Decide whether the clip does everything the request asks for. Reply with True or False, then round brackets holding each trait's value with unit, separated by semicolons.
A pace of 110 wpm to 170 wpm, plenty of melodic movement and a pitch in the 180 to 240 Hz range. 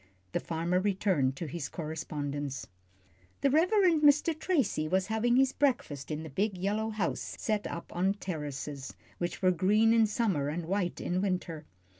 True (160 wpm; 6.0 semitones; 185 Hz)